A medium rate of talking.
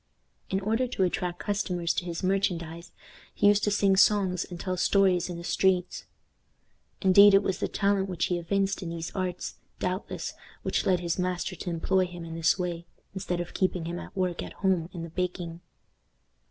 Yes: average, 190 wpm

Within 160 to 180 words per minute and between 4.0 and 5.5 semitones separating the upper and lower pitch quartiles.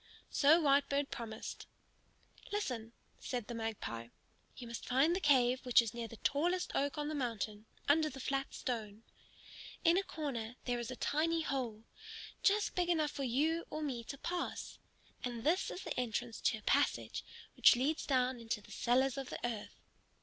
Yes: average, 175 wpm; average, 4.5 semitones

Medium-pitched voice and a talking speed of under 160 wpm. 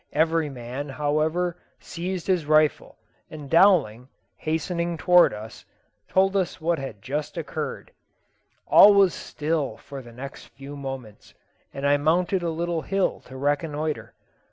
Yes: medium, 155 Hz; slow, 135 wpm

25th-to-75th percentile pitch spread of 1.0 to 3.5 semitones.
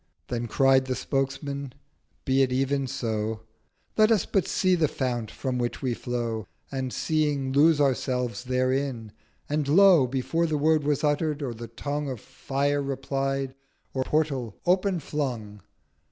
Yes: average, 2.8 semitones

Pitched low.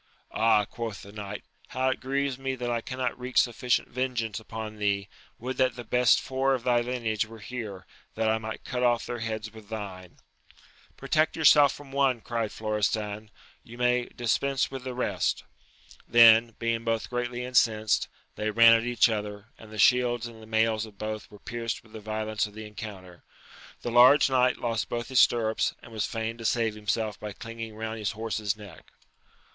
Yes: low, 115 Hz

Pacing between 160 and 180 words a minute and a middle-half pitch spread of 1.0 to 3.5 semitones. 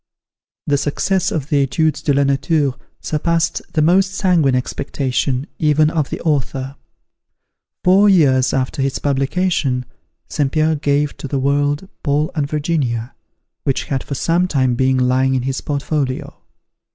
No: average, 145 wpm; average, 2.9 semitones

